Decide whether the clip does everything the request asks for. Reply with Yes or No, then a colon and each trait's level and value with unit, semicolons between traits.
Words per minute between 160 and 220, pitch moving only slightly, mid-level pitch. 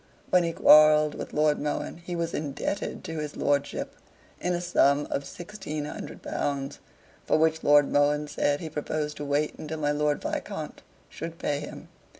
Yes: average, 170 wpm; narrow, 1.7 semitones; medium, 150 Hz